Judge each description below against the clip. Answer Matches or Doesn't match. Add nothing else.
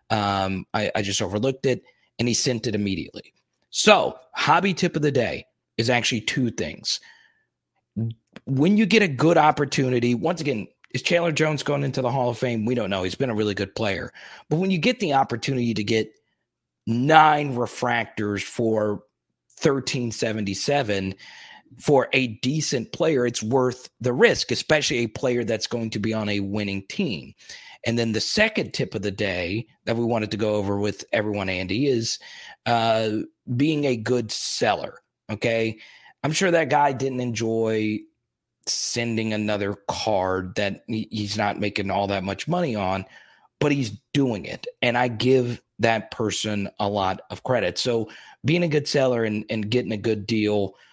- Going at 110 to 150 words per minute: Doesn't match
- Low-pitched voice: Matches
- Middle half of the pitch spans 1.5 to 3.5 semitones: Doesn't match